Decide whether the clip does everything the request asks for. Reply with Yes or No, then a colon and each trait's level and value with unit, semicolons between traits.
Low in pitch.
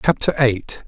Yes: low, 125 Hz